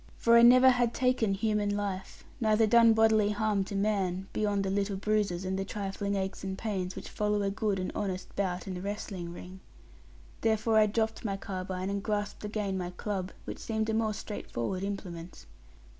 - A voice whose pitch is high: Yes, high, 205 Hz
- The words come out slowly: No, average, 190 wpm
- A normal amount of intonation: No, narrow, 2.2 semitones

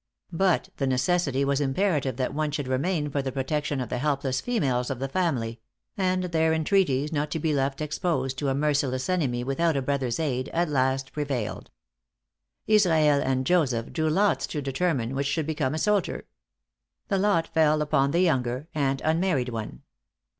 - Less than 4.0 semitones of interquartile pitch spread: Yes, average, 3.6 semitones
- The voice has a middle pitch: Yes, medium, 145 Hz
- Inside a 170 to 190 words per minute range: Yes, average, 175 wpm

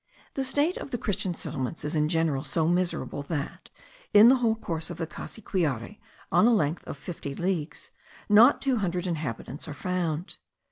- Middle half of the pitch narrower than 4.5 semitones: No, wide, 5.4 semitones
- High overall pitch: No, medium, 175 Hz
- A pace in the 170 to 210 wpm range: Yes, average, 175 wpm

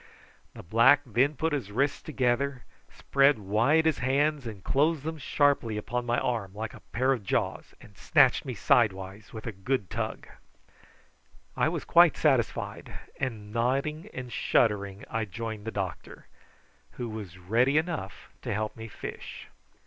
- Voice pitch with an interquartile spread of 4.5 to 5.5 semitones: Yes, average, 4.8 semitones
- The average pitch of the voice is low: Yes, low, 120 Hz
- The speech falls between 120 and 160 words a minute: Yes, average, 155 wpm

